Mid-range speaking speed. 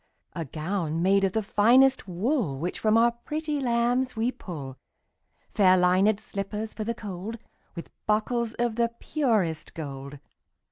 Yes: average, 150 wpm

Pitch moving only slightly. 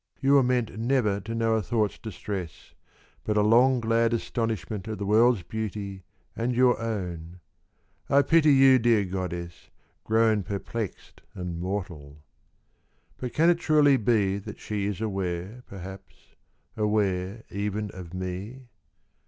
No: average, 3.6 semitones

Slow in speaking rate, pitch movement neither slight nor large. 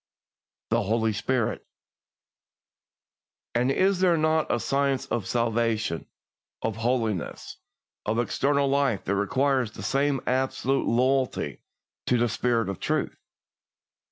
Yes: slow, 115 wpm; average, 3.4 semitones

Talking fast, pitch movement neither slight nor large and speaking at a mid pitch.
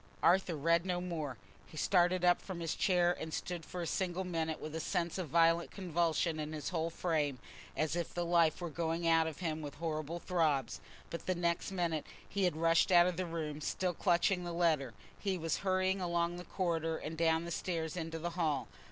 No: fast, 210 wpm; narrow, 1.8 semitones; medium, 170 Hz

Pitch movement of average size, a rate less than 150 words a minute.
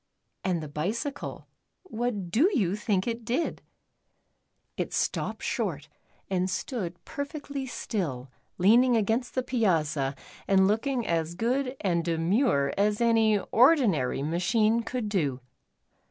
No: wide, 6.1 semitones; average, 140 wpm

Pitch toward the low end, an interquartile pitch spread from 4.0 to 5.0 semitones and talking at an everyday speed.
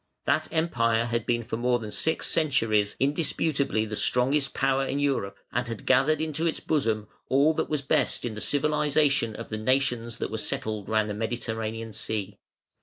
Yes: low, 120 Hz; average, 4.4 semitones; average, 180 wpm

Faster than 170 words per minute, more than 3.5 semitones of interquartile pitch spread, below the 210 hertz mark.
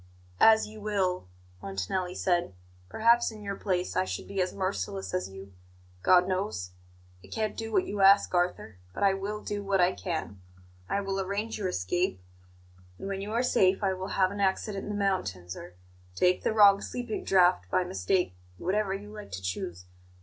No: average, 185 wpm; narrow, 2.6 semitones; high, 190 Hz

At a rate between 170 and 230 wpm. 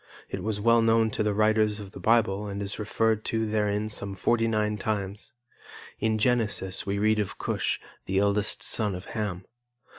Yes: average, 180 wpm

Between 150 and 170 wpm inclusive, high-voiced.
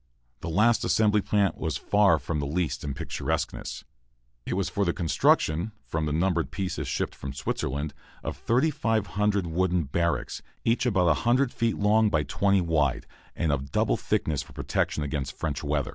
No: average, 160 wpm; very low, 85 Hz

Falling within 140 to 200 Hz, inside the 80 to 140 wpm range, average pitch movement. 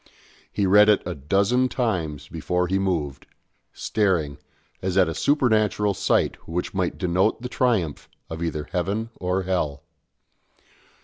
No: very low, 95 Hz; slow, 135 wpm; average, 4.2 semitones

